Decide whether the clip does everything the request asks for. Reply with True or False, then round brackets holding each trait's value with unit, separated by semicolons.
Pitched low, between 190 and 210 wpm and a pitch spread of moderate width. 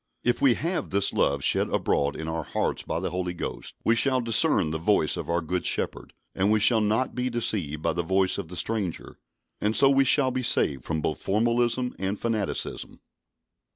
False (105 Hz; 200 wpm; 6.3 semitones)